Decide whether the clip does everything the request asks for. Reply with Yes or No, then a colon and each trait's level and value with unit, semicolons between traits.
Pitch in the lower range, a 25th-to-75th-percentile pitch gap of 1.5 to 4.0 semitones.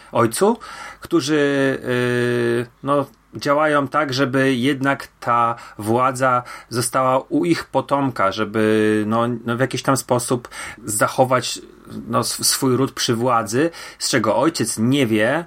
Yes: low, 130 Hz; average, 2.8 semitones